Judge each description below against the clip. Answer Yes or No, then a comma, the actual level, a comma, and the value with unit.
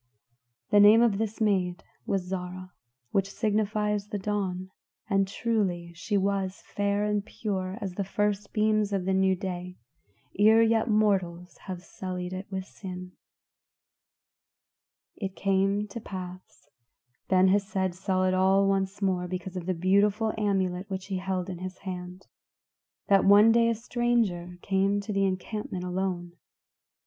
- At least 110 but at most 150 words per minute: Yes, average, 145 wpm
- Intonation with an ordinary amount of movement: No, narrow, 2.0 semitones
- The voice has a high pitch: Yes, high, 195 Hz